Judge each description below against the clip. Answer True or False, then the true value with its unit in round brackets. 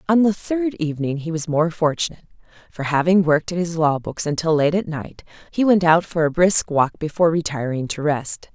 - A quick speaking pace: True (210 wpm)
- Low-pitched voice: False (165 Hz)